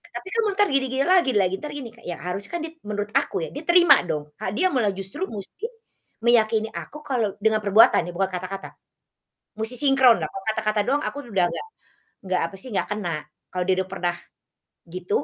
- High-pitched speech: Yes, high, 215 Hz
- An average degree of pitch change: No, wide, 6.0 semitones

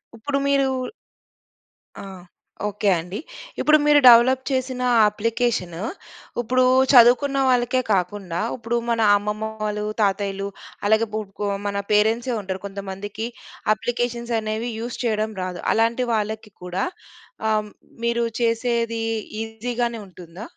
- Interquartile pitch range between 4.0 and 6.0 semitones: No, average, 2.8 semitones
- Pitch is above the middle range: Yes, high, 220 Hz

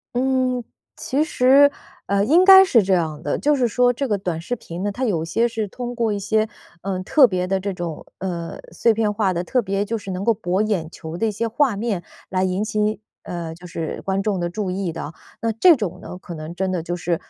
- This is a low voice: No, high, 200 Hz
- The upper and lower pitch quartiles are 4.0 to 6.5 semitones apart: Yes, average, 4.7 semitones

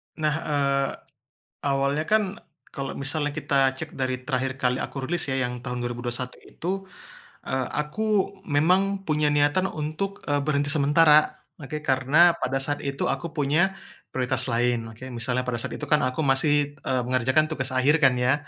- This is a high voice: No, medium, 140 Hz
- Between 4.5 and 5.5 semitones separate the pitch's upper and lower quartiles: No, average, 2.9 semitones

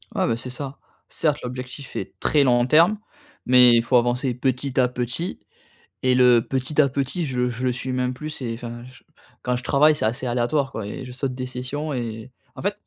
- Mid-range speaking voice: No, low, 125 Hz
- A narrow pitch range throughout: Yes, narrow, 2.0 semitones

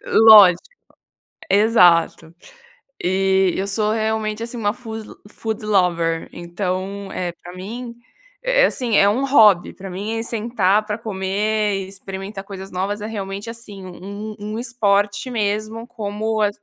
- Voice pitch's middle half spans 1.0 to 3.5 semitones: Yes, narrow, 2.4 semitones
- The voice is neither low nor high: No, high, 205 Hz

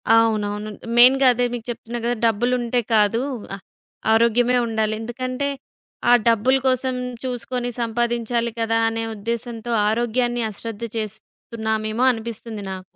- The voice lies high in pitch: Yes, high, 235 Hz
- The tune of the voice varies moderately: No, narrow, 1.7 semitones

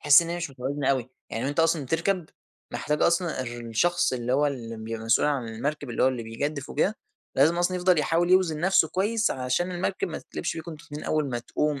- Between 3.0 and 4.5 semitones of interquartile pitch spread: No, average, 5.1 semitones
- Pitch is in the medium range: Yes, medium, 150 Hz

